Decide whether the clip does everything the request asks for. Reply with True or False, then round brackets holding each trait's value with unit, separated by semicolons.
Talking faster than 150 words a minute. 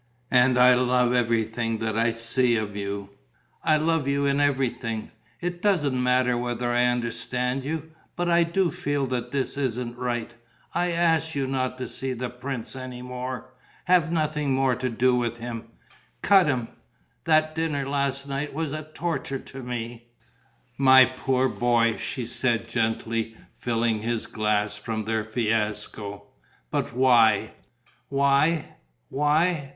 False (145 wpm)